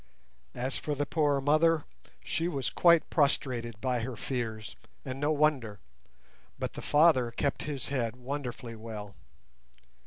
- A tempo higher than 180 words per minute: No, slow, 135 wpm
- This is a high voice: No, low, 135 Hz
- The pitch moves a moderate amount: Yes, average, 3.9 semitones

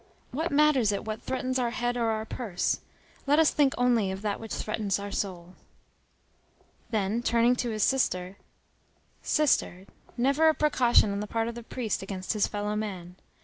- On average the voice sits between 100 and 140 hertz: No, high, 225 Hz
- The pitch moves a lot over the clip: No, average, 3.8 semitones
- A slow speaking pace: No, average, 175 wpm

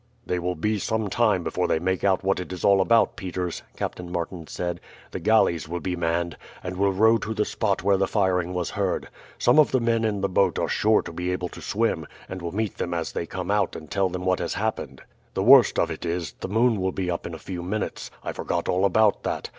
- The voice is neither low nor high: No, very low, 95 Hz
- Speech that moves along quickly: Yes, fast, 250 wpm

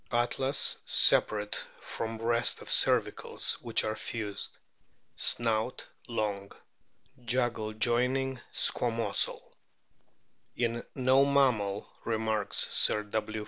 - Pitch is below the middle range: Yes, low, 115 Hz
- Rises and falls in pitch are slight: Yes, narrow, 2.2 semitones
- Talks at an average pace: No, slow, 90 wpm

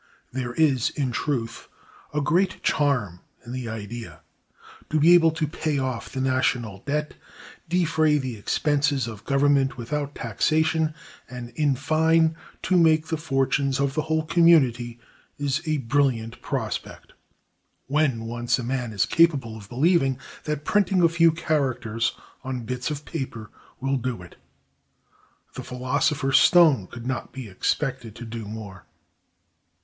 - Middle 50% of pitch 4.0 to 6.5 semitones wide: Yes, average, 4.5 semitones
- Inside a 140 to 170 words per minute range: Yes, average, 145 wpm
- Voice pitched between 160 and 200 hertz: No, low, 135 Hz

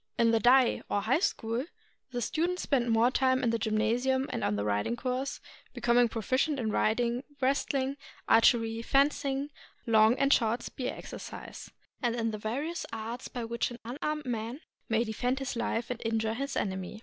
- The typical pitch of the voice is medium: No, high, 240 Hz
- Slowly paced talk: No, average, 175 wpm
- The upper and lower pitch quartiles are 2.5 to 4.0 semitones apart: Yes, average, 2.9 semitones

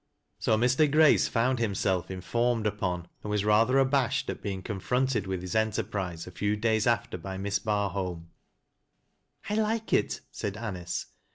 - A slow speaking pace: No, average, 170 wpm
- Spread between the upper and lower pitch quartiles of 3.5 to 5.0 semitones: Yes, average, 4.0 semitones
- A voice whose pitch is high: No, low, 105 Hz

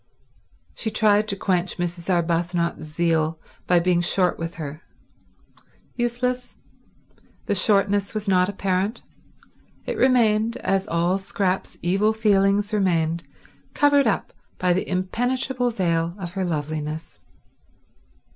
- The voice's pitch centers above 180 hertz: Yes, high, 190 Hz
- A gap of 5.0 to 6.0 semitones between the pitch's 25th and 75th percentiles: No, average, 3.8 semitones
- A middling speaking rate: No, slow, 115 wpm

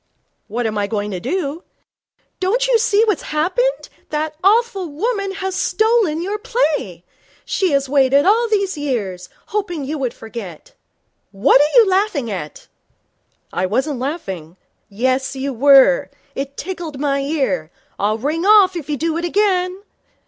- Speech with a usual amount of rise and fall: No, wide, 7.2 semitones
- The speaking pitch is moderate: No, very high, 305 Hz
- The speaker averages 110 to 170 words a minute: Yes, average, 150 wpm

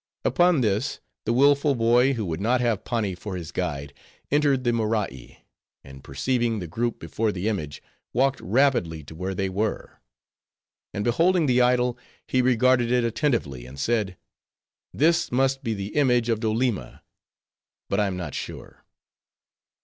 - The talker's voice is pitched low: Yes, low, 115 Hz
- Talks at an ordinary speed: Yes, average, 150 wpm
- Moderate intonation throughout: Yes, average, 5.0 semitones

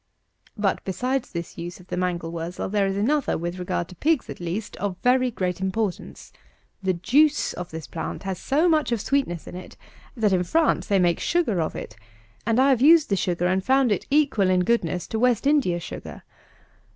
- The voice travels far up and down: Yes, wide, 6.5 semitones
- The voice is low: No, high, 195 Hz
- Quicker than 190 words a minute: Yes, average, 200 wpm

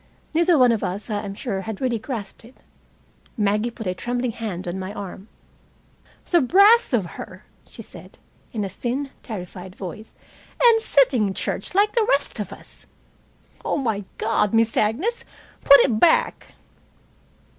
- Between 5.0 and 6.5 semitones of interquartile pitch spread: Yes, wide, 5.4 semitones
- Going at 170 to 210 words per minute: No, average, 155 wpm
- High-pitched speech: Yes, high, 225 Hz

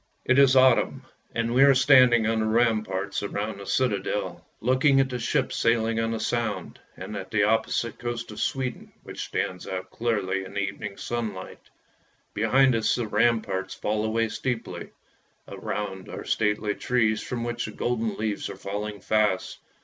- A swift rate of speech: No, average, 170 wpm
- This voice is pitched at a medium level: No, low, 110 Hz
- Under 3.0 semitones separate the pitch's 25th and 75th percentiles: Yes, narrow, 2.6 semitones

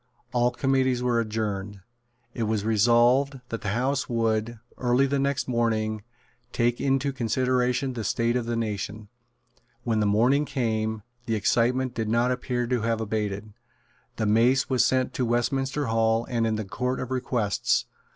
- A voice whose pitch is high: No, low, 120 Hz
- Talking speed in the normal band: Yes, average, 160 wpm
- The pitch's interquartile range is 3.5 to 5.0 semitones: No, narrow, 2.6 semitones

